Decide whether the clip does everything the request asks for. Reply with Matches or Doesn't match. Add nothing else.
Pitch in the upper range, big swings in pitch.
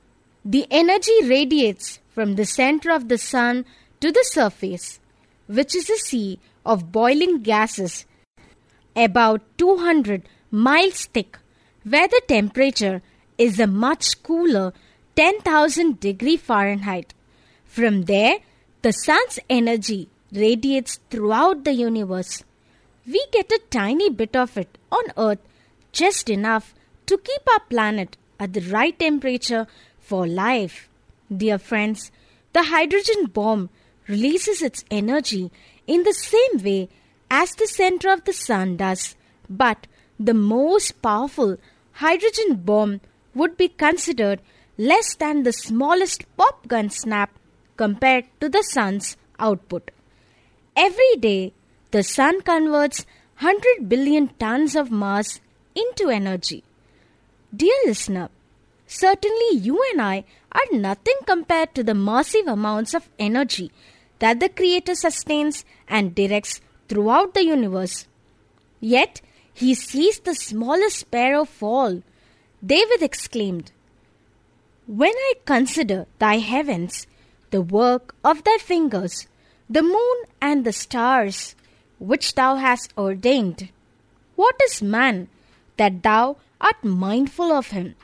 Matches